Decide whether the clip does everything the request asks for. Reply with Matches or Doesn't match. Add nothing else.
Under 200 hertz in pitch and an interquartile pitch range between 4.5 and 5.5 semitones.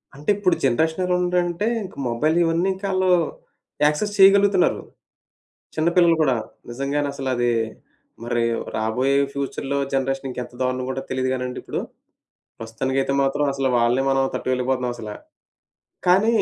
Matches